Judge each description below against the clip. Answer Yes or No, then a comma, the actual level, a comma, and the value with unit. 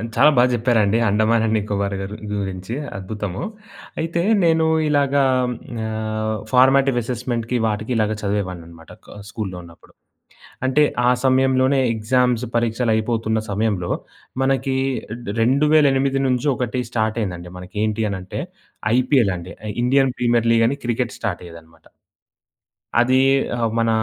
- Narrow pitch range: No, average, 4.0 semitones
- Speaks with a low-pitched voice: Yes, low, 115 Hz